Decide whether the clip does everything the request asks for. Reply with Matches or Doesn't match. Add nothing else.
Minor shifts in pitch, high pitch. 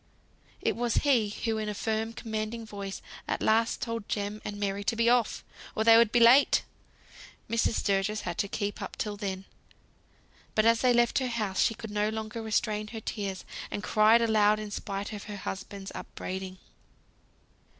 Matches